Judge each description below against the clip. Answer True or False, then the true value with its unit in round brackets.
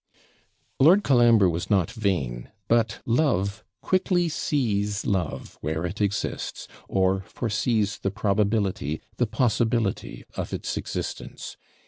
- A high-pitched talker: False (105 Hz)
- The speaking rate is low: True (110 wpm)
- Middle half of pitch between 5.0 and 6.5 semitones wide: False (3.7 semitones)